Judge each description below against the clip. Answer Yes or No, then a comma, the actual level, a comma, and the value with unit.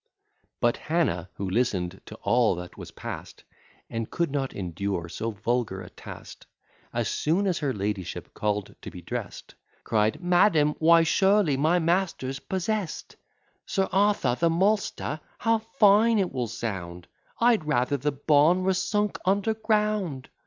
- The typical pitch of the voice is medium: Yes, medium, 150 Hz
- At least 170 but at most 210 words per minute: No, average, 145 wpm